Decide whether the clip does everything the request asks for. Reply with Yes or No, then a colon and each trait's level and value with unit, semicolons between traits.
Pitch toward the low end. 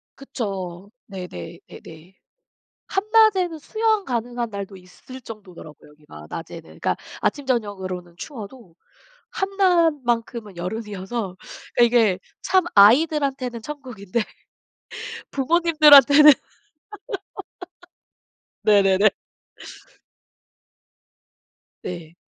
No: high, 230 Hz